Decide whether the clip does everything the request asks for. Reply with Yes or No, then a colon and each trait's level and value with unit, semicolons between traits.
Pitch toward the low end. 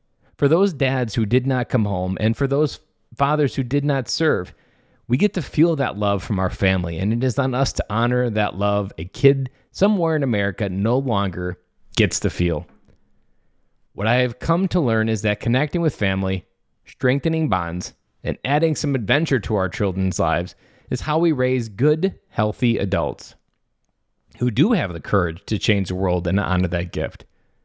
Yes: low, 115 Hz